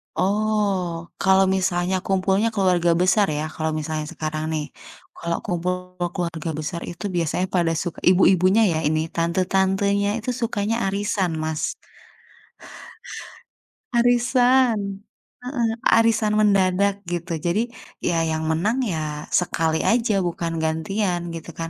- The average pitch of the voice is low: No, medium, 185 Hz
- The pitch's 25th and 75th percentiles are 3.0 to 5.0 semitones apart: Yes, average, 3.5 semitones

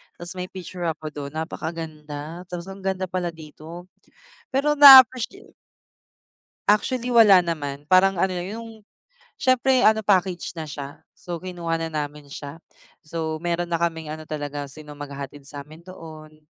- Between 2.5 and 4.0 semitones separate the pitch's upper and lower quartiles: Yes, average, 3.5 semitones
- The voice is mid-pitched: Yes, medium, 170 Hz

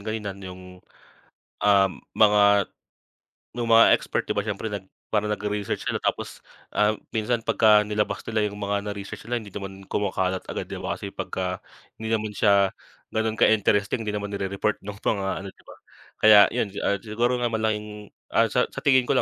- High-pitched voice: No, low, 105 Hz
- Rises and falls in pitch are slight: Yes, narrow, 1.6 semitones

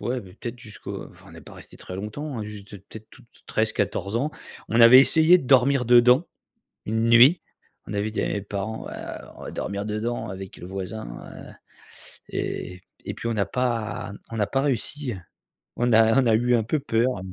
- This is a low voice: Yes, low, 115 Hz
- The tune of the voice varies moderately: Yes, average, 3.2 semitones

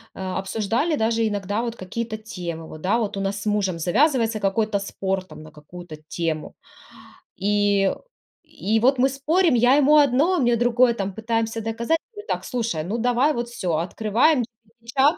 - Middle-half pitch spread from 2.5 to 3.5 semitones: No, average, 3.9 semitones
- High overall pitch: Yes, high, 225 Hz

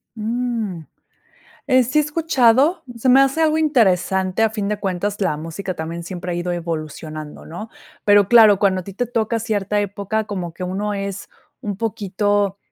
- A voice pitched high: Yes, high, 205 Hz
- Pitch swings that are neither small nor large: Yes, average, 3.8 semitones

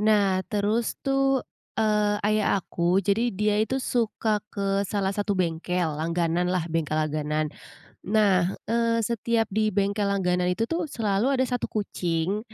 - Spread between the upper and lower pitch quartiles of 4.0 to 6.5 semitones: No, average, 3.5 semitones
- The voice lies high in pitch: Yes, high, 205 Hz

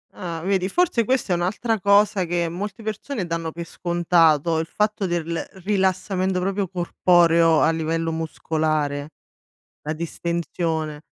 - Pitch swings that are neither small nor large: Yes, average, 3.0 semitones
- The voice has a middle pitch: Yes, medium, 175 Hz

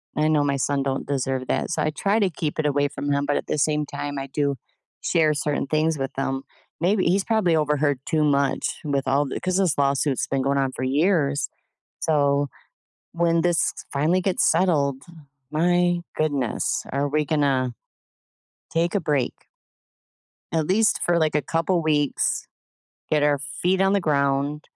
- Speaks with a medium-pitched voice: Yes, medium, 150 Hz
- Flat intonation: No, average, 3.0 semitones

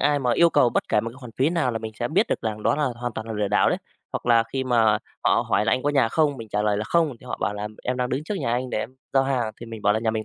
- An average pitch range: Yes, average, 3.4 semitones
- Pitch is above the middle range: No, low, 120 Hz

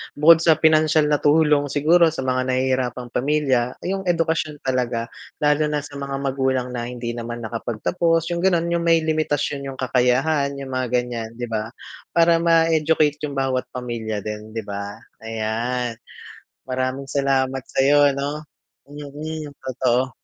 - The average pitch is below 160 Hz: Yes, low, 135 Hz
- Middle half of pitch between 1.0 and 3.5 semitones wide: No, average, 3.9 semitones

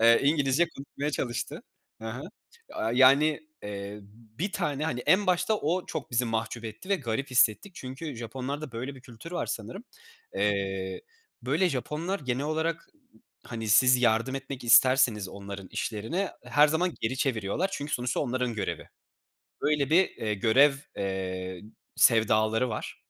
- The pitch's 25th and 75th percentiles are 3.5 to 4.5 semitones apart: No, average, 5.1 semitones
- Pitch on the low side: Yes, low, 125 Hz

